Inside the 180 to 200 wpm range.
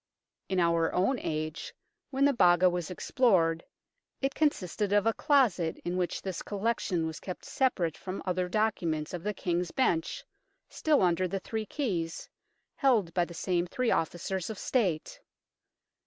No: average, 155 wpm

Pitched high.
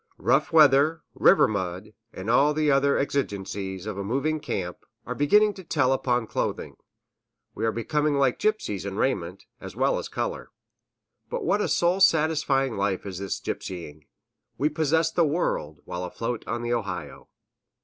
No: low, 135 Hz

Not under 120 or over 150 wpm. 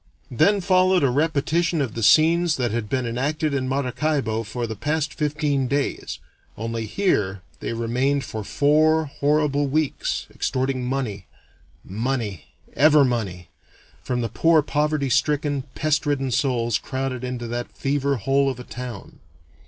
Yes: average, 145 wpm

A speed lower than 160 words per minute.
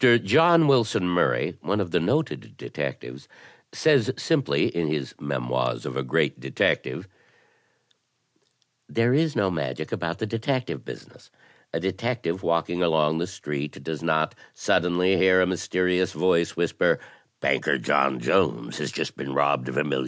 Yes: average, 145 wpm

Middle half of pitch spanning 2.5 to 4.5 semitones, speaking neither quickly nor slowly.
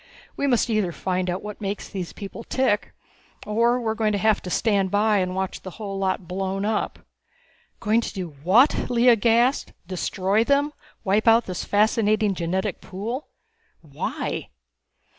Yes: average, 3.1 semitones; average, 160 wpm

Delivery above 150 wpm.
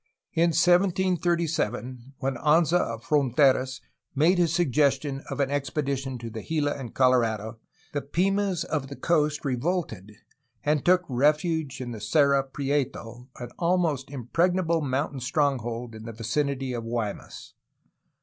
No: slow, 135 wpm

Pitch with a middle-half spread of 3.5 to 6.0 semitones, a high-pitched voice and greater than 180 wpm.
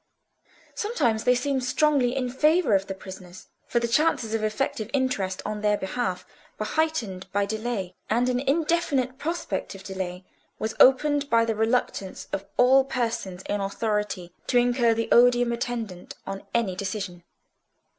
No: average, 4.5 semitones; high, 230 Hz; average, 155 wpm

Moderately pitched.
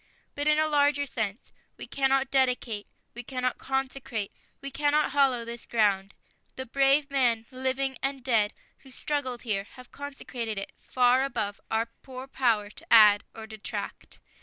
No: very high, 255 Hz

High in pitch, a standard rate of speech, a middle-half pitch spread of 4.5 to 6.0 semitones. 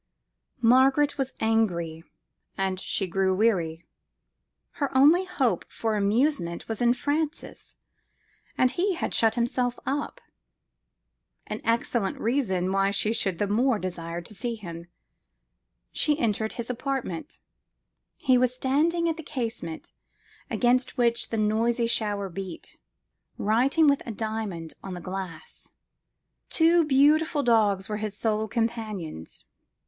No: high, 225 Hz; slow, 125 wpm; average, 5.3 semitones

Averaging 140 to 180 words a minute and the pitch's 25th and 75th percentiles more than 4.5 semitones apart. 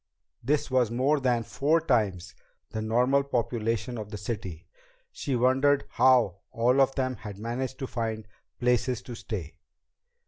No: average, 145 wpm; average, 3.2 semitones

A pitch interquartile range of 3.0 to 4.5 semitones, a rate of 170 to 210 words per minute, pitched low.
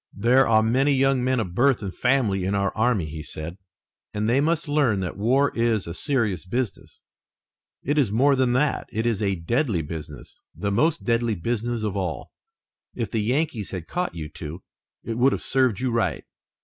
No: average, 5.1 semitones; average, 190 wpm; low, 115 Hz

